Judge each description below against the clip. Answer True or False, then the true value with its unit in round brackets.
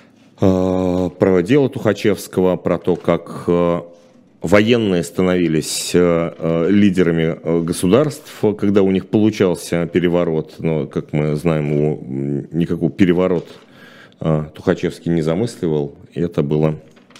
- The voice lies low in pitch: True (85 Hz)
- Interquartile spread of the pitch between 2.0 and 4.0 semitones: True (2.6 semitones)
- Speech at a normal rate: False (100 wpm)